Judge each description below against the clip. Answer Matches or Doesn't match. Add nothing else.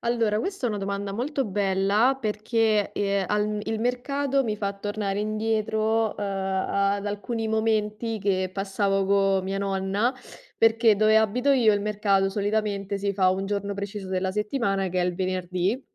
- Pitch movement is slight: Matches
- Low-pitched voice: Doesn't match